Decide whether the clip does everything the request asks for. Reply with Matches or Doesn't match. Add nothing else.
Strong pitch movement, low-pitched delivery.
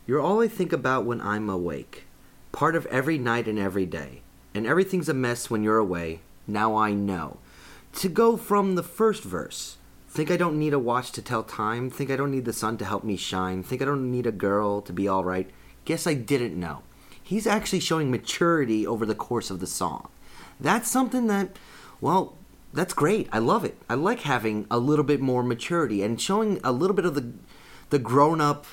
Matches